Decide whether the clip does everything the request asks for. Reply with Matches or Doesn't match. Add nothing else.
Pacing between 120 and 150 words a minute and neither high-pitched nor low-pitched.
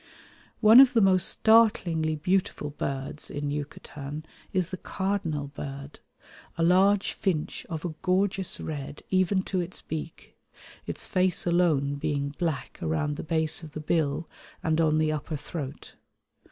Matches